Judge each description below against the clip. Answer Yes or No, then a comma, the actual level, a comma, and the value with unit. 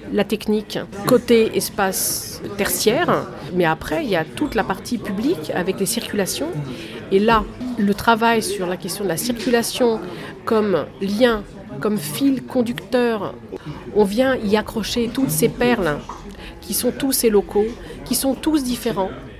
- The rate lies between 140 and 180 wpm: Yes, average, 150 wpm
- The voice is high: Yes, high, 220 Hz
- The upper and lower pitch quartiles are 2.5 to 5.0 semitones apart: Yes, average, 3.9 semitones